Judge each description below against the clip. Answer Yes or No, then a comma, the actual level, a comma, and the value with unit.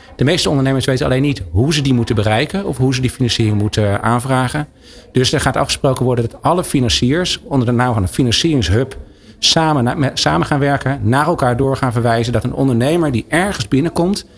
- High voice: No, low, 130 Hz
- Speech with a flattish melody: No, average, 3.3 semitones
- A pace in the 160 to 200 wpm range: Yes, average, 195 wpm